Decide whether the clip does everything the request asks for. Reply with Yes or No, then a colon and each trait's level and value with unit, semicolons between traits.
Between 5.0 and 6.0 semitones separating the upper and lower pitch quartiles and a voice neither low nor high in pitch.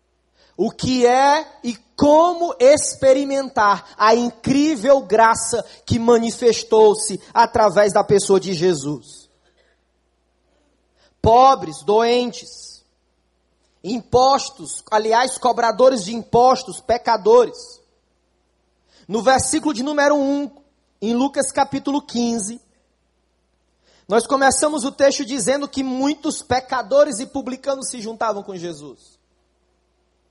No: wide, 5.4 semitones; high, 240 Hz